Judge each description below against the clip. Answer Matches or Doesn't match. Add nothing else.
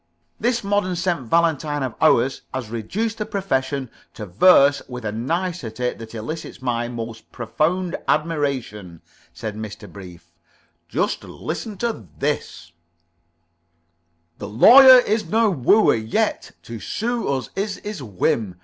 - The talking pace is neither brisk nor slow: Doesn't match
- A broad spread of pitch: Matches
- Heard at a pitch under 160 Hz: Matches